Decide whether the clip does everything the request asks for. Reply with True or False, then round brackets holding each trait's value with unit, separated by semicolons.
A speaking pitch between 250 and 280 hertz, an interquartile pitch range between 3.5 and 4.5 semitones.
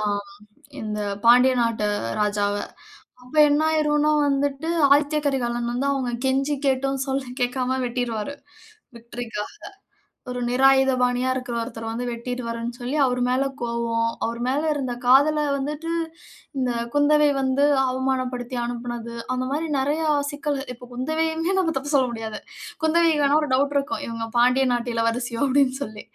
False (255 Hz; 3.1 semitones)